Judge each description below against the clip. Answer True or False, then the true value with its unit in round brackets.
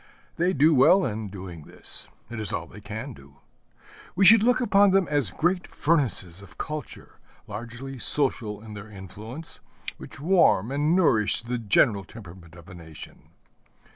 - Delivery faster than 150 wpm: True (160 wpm)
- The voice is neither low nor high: False (115 Hz)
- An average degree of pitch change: False (7.7 semitones)